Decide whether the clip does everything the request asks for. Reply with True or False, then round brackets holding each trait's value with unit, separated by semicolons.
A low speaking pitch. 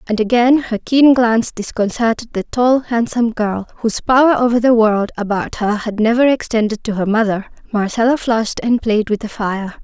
False (225 Hz)